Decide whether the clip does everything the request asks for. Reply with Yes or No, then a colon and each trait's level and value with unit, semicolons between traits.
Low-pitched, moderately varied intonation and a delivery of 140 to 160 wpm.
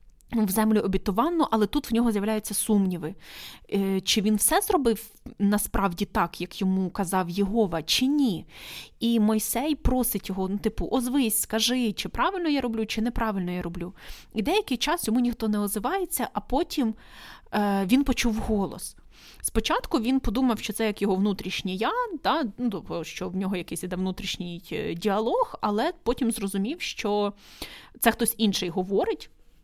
No: high, 215 Hz; average, 3.9 semitones; average, 150 wpm